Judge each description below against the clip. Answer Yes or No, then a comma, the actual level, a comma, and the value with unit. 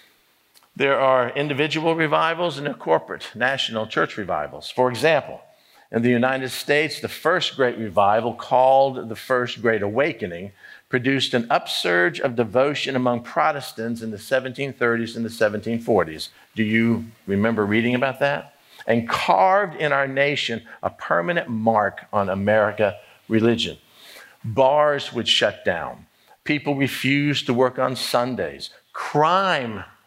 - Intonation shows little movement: No, average, 3.6 semitones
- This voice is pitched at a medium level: No, low, 125 Hz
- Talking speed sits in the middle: No, slow, 130 wpm